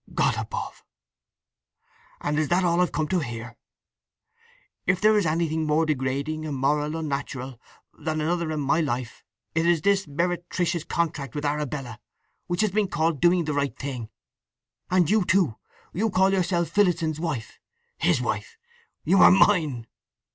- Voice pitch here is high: No, medium, 160 Hz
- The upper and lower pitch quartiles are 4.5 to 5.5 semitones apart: No, average, 3.7 semitones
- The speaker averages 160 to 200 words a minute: No, average, 145 wpm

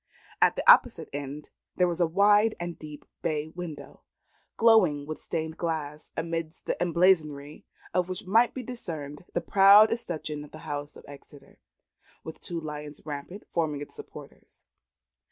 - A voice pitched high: No, medium, 160 Hz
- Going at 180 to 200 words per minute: No, average, 155 wpm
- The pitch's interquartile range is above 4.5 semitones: No, average, 3.5 semitones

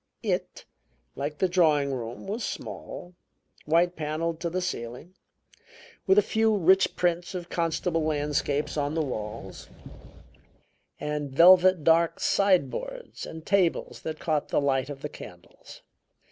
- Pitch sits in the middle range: Yes, medium, 160 Hz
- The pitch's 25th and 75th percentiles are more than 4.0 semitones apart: No, average, 3.7 semitones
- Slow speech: Yes, slow, 130 wpm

